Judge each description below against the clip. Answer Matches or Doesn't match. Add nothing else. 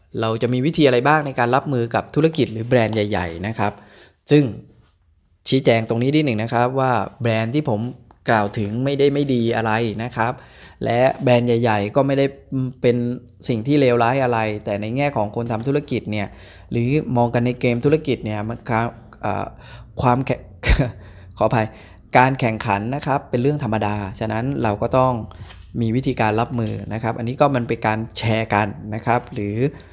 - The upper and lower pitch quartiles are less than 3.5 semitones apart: Matches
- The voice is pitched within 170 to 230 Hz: Doesn't match